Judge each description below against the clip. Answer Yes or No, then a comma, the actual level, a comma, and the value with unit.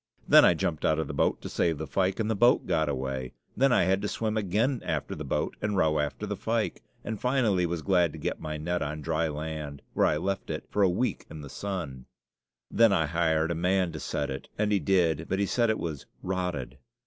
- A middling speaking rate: No, fast, 240 wpm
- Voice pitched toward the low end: Yes, very low, 85 Hz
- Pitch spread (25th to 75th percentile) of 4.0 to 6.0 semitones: Yes, average, 4.4 semitones